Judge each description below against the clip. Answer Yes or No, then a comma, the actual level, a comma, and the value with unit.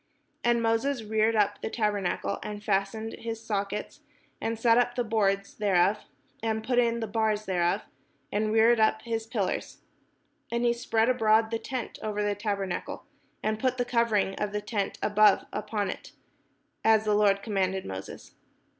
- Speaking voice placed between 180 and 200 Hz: No, high, 215 Hz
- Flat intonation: Yes, narrow, 1.9 semitones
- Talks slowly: No, average, 165 wpm